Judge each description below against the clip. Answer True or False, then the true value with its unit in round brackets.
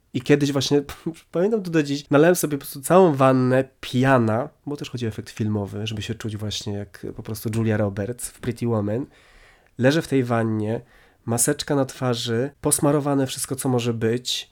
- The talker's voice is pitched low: True (130 Hz)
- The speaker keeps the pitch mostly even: False (4.2 semitones)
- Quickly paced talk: True (185 wpm)